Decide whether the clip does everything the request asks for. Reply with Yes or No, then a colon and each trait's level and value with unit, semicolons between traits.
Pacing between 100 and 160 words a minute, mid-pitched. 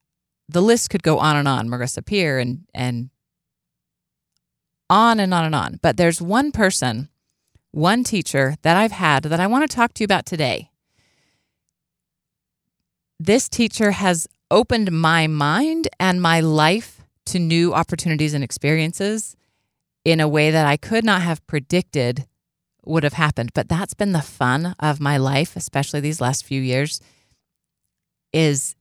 Yes: average, 155 wpm; medium, 160 Hz